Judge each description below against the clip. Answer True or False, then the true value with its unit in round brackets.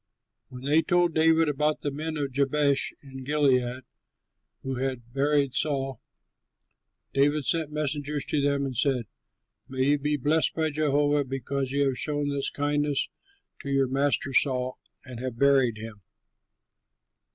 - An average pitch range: False (1.9 semitones)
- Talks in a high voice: False (140 Hz)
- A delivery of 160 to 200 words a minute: False (145 wpm)